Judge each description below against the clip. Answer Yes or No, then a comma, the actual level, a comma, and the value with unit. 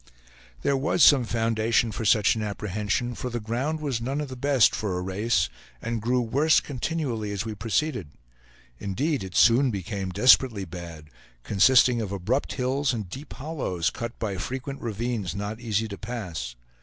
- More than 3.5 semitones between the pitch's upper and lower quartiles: Yes, average, 4.4 semitones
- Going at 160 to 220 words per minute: Yes, average, 170 wpm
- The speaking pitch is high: No, low, 115 Hz